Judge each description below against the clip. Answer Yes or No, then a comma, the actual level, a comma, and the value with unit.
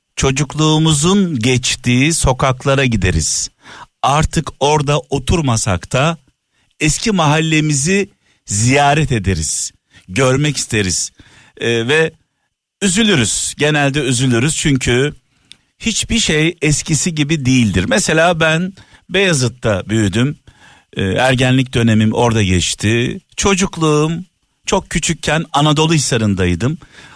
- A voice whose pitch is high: No, medium, 140 Hz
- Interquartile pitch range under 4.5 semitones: No, average, 5.2 semitones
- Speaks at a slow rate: Yes, slow, 85 wpm